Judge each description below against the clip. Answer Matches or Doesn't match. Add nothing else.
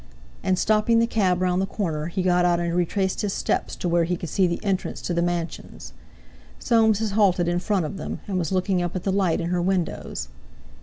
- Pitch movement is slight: Matches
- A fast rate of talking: Matches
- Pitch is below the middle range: Doesn't match